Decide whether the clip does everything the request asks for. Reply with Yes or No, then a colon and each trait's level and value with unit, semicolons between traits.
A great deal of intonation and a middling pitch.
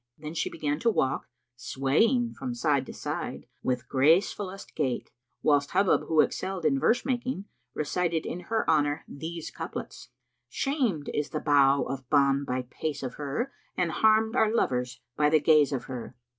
Yes: wide, 6.1 semitones; medium, 155 Hz